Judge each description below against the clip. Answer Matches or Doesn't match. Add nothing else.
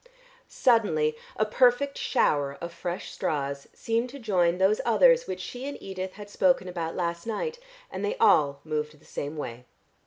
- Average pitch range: Doesn't match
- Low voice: Doesn't match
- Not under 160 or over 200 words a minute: Matches